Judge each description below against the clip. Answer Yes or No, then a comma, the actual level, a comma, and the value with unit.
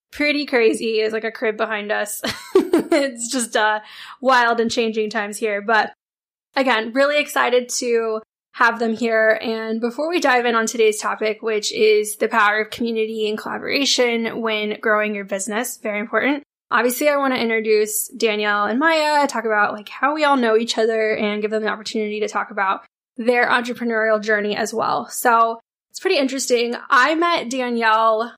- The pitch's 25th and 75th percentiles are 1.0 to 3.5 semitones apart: Yes, narrow, 2.6 semitones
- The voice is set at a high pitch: Yes, high, 225 Hz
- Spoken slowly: No, average, 175 wpm